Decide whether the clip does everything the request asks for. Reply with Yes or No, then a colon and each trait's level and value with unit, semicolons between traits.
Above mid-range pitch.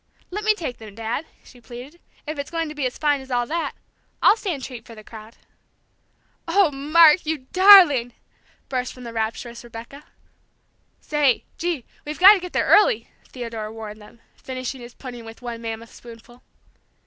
Yes: very high, 255 Hz